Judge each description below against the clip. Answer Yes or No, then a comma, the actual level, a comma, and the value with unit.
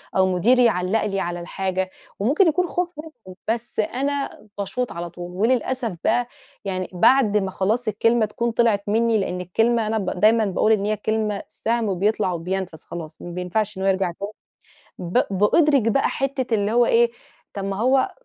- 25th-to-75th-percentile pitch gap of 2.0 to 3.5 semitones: No, average, 4.0 semitones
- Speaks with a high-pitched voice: Yes, high, 215 Hz